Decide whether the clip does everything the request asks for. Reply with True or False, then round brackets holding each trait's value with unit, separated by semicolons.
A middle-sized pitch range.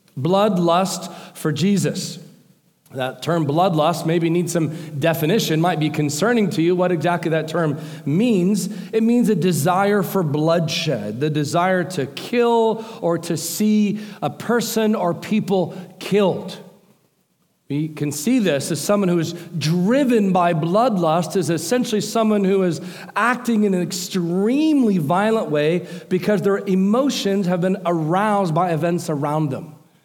True (3.6 semitones)